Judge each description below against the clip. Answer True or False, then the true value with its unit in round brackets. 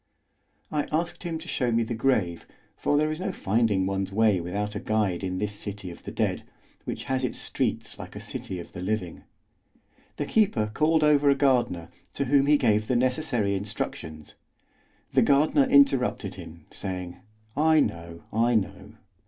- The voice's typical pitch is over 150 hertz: False (115 Hz)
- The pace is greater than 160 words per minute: True (175 wpm)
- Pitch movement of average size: False (7.1 semitones)